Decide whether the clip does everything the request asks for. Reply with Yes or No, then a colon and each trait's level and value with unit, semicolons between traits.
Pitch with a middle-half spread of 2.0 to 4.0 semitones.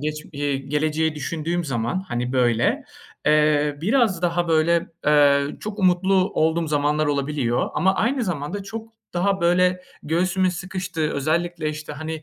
Yes: average, 3.6 semitones